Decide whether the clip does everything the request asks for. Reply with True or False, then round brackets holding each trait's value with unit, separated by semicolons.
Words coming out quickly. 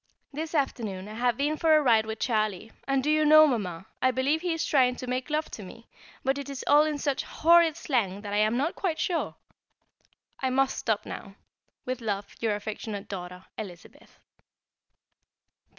False (190 wpm)